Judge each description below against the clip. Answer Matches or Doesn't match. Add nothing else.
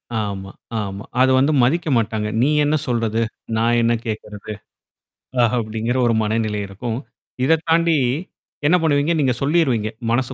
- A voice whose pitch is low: Matches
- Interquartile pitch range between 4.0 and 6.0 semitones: Matches